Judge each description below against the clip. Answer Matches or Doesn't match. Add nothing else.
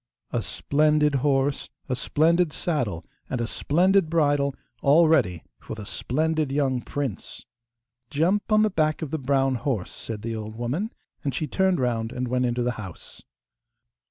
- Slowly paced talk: Doesn't match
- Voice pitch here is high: Doesn't match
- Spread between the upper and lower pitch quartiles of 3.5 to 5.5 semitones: Matches